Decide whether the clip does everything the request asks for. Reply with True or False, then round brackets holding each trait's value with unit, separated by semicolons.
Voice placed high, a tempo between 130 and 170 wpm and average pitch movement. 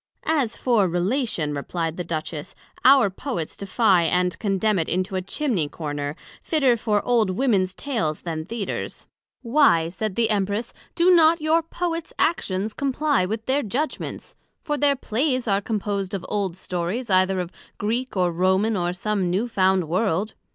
False (205 Hz; 160 wpm; 5.7 semitones)